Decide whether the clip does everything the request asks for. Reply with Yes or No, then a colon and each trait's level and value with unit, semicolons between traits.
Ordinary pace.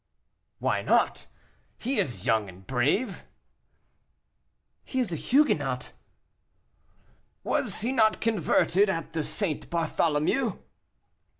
No: slow, 100 wpm